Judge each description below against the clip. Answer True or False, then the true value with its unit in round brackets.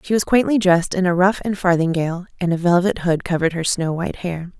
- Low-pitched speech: False (180 Hz)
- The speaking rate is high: True (235 wpm)